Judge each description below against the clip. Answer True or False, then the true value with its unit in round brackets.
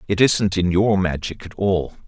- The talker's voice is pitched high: False (95 Hz)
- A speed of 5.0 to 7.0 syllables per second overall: False (4.4 syllables/s)